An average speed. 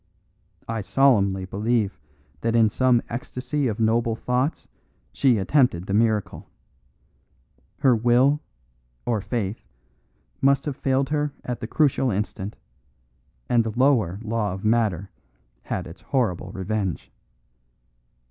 No: slow, 120 wpm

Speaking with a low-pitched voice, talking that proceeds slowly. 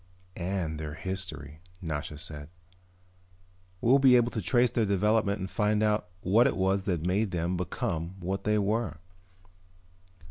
No: very low, 95 Hz; average, 145 wpm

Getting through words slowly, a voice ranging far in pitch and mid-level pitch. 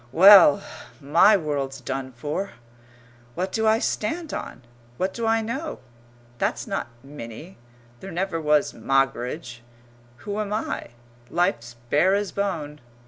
Yes: slow, 130 wpm; wide, 6.8 semitones; medium, 170 Hz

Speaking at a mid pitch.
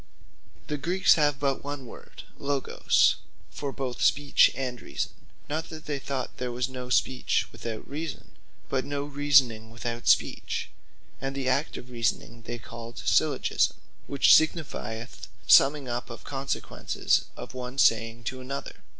No: low, 130 Hz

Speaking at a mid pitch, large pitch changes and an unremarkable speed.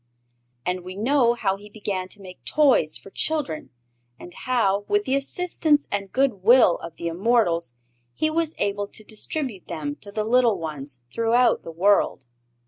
No: high, 205 Hz; wide, 5.8 semitones; average, 160 wpm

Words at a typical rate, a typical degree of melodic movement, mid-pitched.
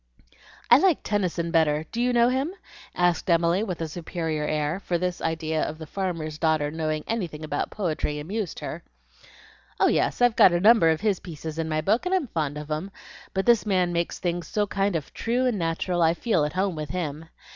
No: fast, 210 wpm; average, 4.5 semitones; medium, 170 Hz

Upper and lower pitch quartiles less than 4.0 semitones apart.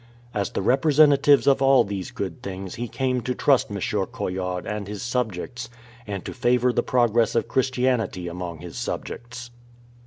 No: average, 4.7 semitones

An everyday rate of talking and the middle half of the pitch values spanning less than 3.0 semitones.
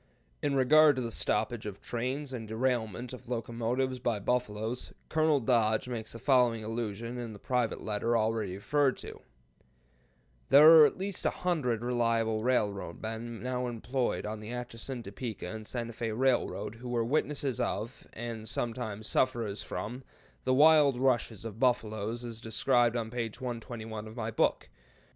Yes: average, 155 wpm; narrow, 2.5 semitones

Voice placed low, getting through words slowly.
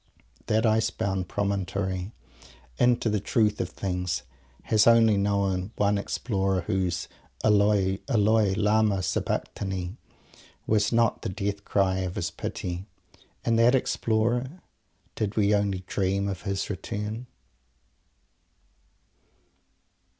Yes: low, 100 Hz; slow, 110 wpm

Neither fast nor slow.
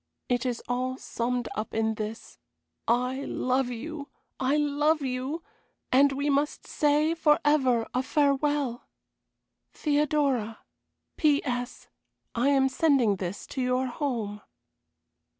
No: slow, 115 wpm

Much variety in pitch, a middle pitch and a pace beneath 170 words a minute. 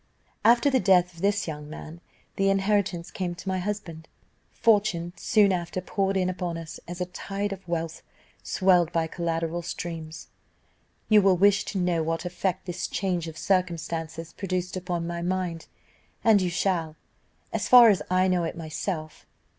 No: narrow, 2.6 semitones; medium, 180 Hz; average, 160 wpm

